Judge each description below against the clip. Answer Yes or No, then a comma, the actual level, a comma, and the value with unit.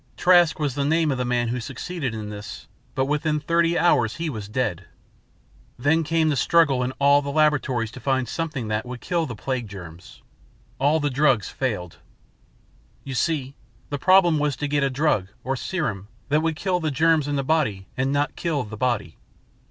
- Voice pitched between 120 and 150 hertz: Yes, medium, 140 Hz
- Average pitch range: Yes, average, 4.4 semitones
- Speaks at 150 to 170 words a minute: No, average, 190 wpm